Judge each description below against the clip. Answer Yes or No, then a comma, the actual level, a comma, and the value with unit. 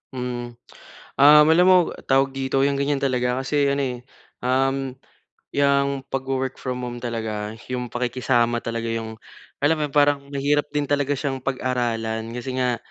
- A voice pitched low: Yes, low, 130 Hz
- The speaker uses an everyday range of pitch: No, narrow, 2.3 semitones